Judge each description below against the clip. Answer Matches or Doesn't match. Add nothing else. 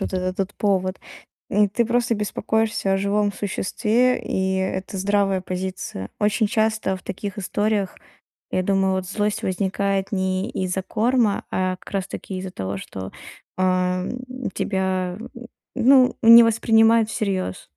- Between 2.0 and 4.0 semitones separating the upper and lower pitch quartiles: Matches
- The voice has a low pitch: Doesn't match